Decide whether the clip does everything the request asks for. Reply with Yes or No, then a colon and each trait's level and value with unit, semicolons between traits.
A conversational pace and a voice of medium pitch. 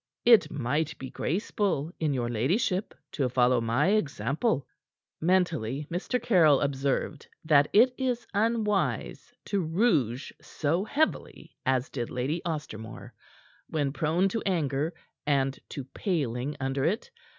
No: slow, 125 wpm; medium, 150 Hz